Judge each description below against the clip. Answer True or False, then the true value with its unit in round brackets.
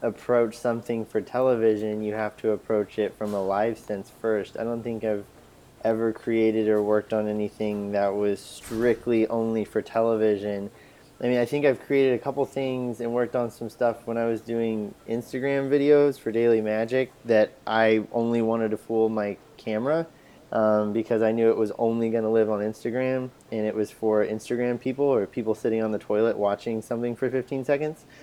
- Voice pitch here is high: False (115 Hz)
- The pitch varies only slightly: True (2.1 semitones)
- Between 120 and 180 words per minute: False (190 wpm)